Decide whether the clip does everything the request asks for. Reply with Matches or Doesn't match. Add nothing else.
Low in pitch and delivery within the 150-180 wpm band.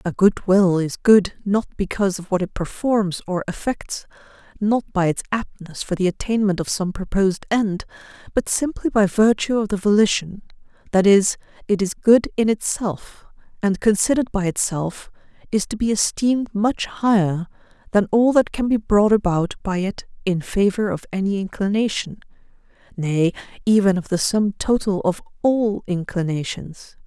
Doesn't match